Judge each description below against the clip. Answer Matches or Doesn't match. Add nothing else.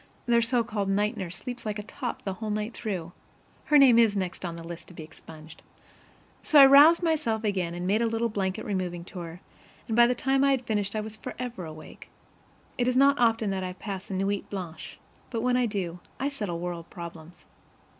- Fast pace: Matches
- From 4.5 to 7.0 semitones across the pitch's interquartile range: Matches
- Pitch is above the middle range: Matches